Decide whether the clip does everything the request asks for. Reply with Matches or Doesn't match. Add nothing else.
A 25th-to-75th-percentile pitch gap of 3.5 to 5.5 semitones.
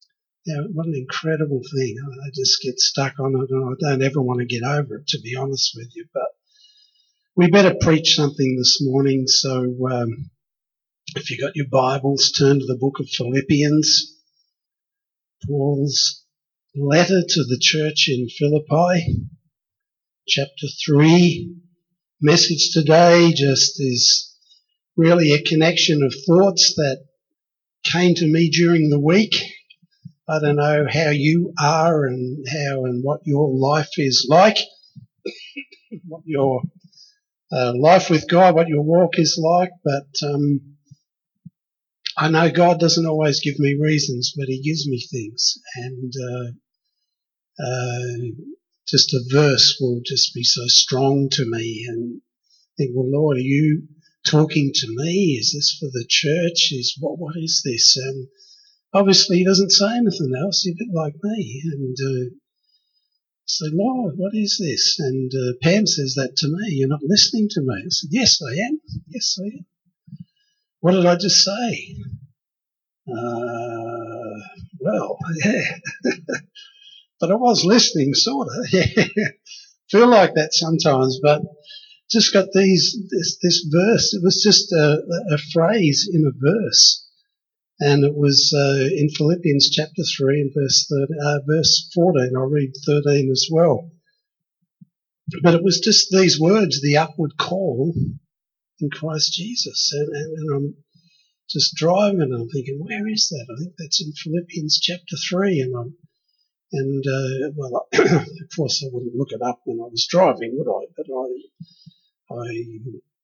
Matches